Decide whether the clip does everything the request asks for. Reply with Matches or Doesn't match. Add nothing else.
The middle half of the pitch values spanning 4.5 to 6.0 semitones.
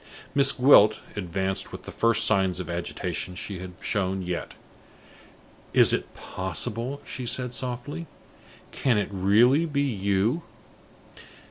Matches